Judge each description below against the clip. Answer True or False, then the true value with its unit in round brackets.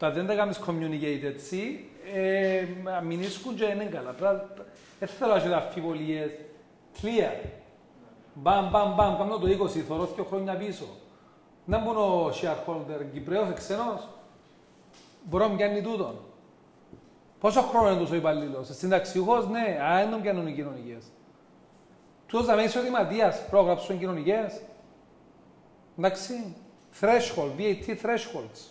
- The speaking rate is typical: False (85 wpm)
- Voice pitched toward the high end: True (195 Hz)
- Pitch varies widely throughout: False (3.8 semitones)